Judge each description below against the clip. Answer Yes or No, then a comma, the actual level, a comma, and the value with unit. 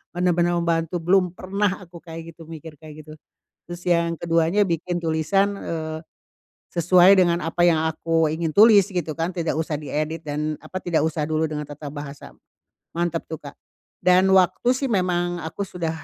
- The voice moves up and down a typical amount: No, narrow, 2.2 semitones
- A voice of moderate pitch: Yes, medium, 170 Hz